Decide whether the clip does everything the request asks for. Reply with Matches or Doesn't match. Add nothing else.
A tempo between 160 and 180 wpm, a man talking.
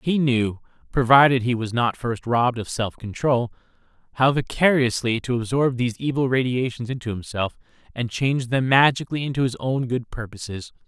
Doesn't match